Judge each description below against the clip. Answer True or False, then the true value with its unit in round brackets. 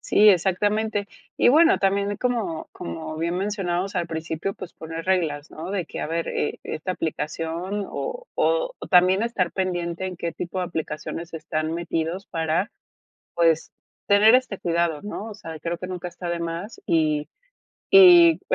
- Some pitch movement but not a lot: True (3.7 semitones)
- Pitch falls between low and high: True (180 Hz)